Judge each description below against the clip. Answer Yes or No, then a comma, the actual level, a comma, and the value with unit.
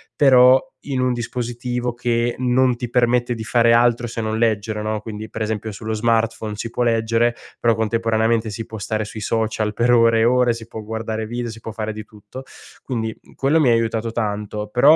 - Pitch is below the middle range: Yes, low, 115 Hz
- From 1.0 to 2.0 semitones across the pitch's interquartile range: Yes, narrow, 1.7 semitones